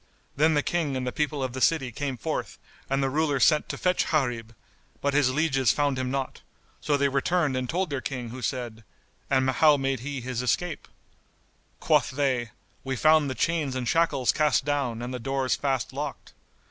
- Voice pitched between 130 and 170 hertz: Yes, low, 135 Hz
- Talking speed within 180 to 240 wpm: Yes, average, 195 wpm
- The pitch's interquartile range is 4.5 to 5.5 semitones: No, narrow, 2.5 semitones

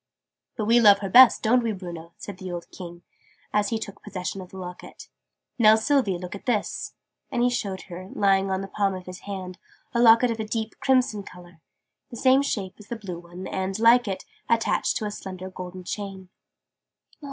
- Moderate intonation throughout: Yes, average, 3.4 semitones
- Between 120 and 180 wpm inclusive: No, average, 200 wpm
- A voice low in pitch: No, high, 195 Hz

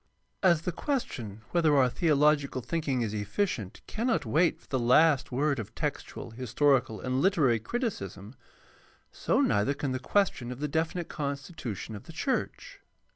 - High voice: No, medium, 140 Hz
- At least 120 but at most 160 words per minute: Yes, average, 150 wpm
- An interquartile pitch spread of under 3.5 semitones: No, wide, 5.6 semitones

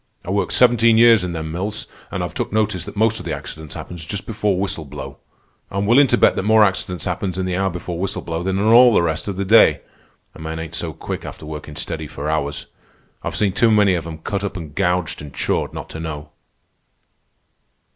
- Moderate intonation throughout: Yes, average, 4.6 semitones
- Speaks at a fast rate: Yes, fast, 225 wpm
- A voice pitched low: Yes, very low, 90 Hz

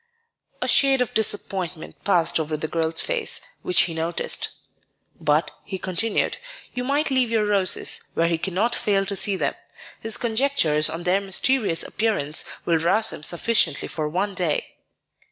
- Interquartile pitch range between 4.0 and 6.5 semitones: Yes, average, 5.2 semitones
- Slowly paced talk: No, average, 155 wpm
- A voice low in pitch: No, high, 190 Hz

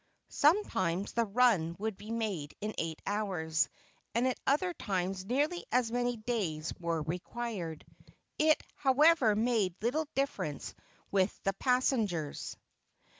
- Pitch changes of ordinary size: No, wide, 5.8 semitones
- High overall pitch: Yes, high, 215 Hz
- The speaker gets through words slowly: Yes, slow, 125 wpm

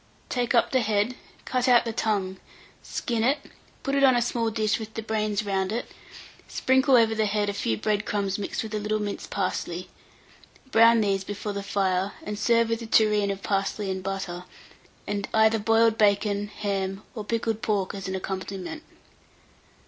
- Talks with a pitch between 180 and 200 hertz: No, high, 210 Hz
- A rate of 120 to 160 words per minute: No, average, 180 wpm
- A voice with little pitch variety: Yes, narrow, 2.3 semitones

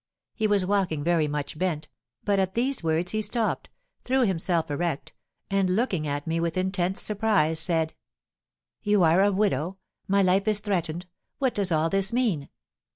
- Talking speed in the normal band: Yes, average, 165 wpm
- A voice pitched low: No, medium, 185 Hz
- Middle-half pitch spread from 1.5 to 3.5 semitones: No, average, 4.0 semitones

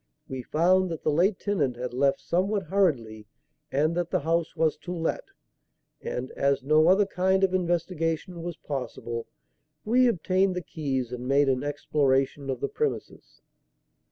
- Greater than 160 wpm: No, average, 155 wpm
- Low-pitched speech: No, medium, 160 Hz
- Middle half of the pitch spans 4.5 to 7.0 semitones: Yes, average, 5.1 semitones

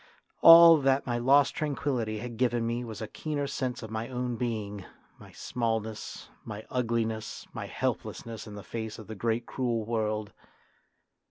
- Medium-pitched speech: No, low, 115 Hz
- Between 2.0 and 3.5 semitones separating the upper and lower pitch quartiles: Yes, narrow, 2.4 semitones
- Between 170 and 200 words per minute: No, average, 160 wpm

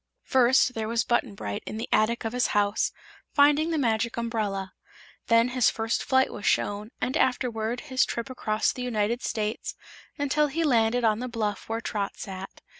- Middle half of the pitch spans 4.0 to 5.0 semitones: No, average, 2.8 semitones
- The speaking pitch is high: Yes, high, 230 Hz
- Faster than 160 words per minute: Yes, average, 180 wpm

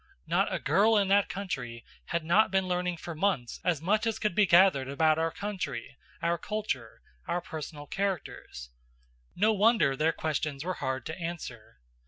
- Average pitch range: No, wide, 5.7 semitones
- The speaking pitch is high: No, medium, 170 Hz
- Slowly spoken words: No, average, 170 wpm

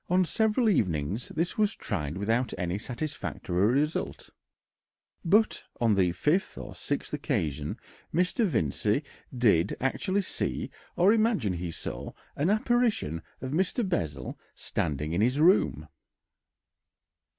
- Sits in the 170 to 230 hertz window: No, low, 130 Hz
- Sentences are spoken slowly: Yes, slow, 120 wpm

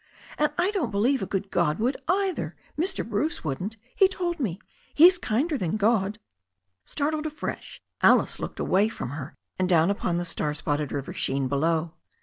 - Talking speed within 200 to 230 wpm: No, average, 170 wpm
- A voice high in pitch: Yes, high, 205 Hz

